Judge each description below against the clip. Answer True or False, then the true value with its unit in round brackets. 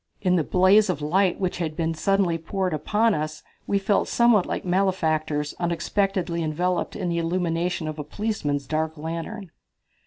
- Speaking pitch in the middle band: True (175 Hz)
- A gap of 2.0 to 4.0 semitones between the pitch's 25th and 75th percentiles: True (3.5 semitones)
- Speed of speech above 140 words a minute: True (160 wpm)